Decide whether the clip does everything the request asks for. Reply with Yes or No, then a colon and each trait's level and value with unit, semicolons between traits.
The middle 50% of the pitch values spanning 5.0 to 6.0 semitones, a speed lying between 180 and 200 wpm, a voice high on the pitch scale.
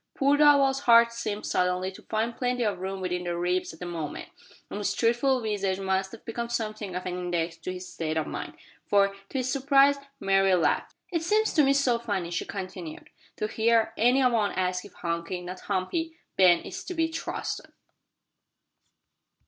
Yes: average, 5.3 semitones; average, 185 wpm; high, 205 Hz